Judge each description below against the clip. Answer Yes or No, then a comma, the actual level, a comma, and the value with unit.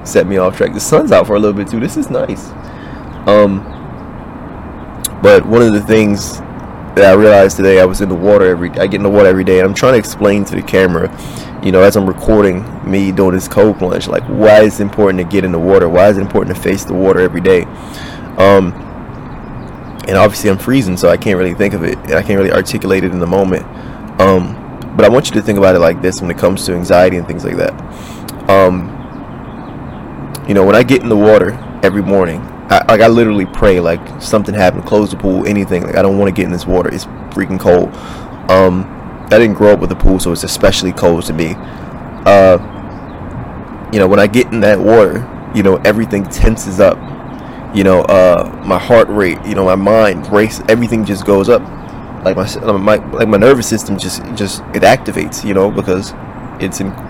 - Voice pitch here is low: Yes, very low, 95 Hz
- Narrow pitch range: Yes, narrow, 2.1 semitones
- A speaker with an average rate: No, fast, 220 wpm